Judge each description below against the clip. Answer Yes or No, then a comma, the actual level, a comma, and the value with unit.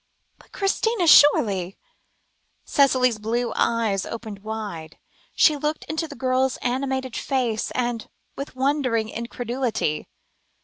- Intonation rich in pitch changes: No, average, 3.9 semitones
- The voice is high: Yes, high, 245 Hz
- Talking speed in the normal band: No, slow, 100 wpm